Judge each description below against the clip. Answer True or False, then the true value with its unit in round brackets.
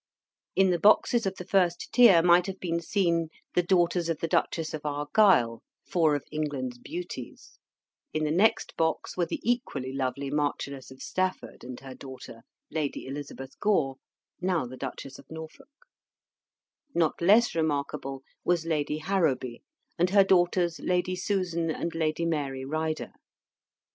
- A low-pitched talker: False (160 Hz)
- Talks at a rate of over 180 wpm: False (150 wpm)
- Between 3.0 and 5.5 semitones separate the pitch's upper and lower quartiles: True (4.2 semitones)